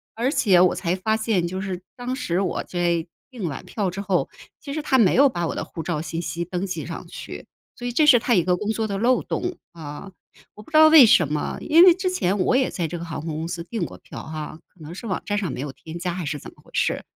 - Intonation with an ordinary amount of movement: No, wide, 5.9 semitones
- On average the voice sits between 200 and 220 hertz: No, medium, 185 Hz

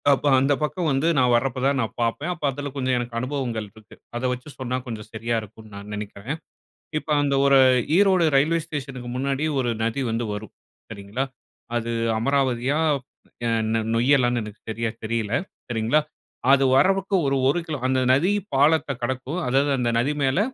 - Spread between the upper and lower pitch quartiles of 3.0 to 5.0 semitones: Yes, average, 3.5 semitones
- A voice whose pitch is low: Yes, low, 130 Hz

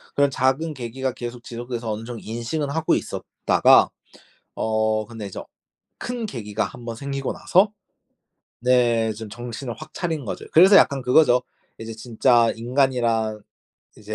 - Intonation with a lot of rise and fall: No, average, 3.3 semitones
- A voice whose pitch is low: Yes, low, 120 Hz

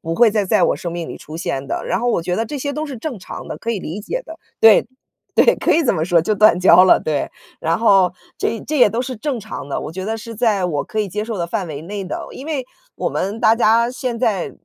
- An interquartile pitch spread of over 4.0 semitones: Yes, average, 5.0 semitones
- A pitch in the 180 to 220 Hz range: Yes, high, 210 Hz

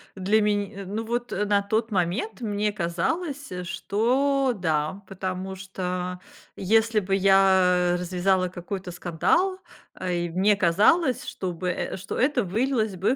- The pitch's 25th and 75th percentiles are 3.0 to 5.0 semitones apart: Yes, average, 3.4 semitones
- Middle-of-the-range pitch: No, high, 195 Hz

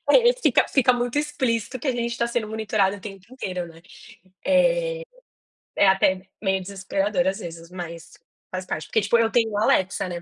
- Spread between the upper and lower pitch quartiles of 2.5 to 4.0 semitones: No, average, 4.5 semitones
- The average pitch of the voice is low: No, high, 210 Hz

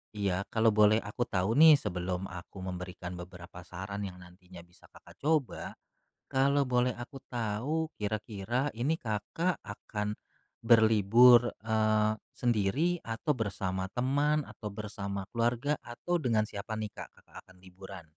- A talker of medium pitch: No, low, 110 Hz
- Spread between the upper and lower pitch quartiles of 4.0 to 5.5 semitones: Yes, average, 4.4 semitones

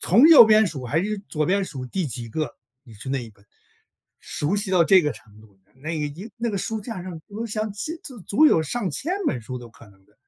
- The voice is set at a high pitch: No, medium, 170 Hz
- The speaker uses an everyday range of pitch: No, wide, 8.8 semitones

